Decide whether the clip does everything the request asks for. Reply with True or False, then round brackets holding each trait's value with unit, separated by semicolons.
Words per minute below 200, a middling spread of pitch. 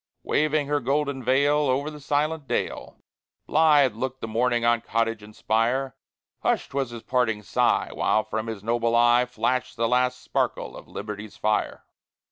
True (160 wpm; 3.5 semitones)